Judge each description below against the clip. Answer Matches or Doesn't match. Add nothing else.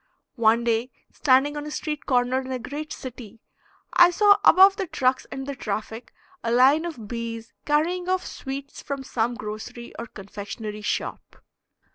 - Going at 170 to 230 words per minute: Doesn't match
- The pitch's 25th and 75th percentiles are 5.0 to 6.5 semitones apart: Doesn't match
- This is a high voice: Matches